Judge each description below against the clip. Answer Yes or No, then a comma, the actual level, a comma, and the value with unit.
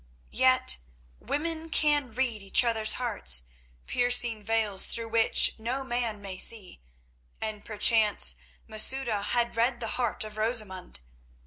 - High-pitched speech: Yes, high, 225 Hz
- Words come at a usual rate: No, slow, 125 wpm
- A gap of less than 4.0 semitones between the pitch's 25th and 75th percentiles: Yes, narrow, 2.5 semitones